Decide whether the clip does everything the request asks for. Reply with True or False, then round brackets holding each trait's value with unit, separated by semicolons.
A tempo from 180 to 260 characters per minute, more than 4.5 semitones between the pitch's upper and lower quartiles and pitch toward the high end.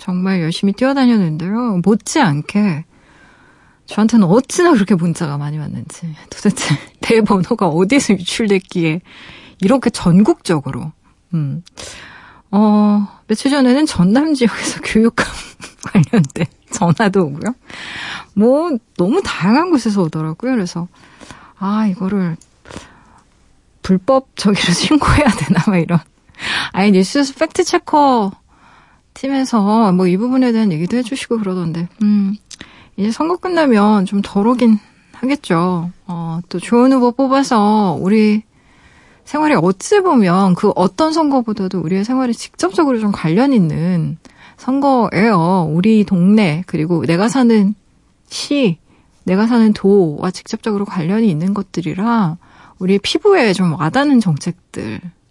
False (275 characters per minute; 5.4 semitones; 205 Hz)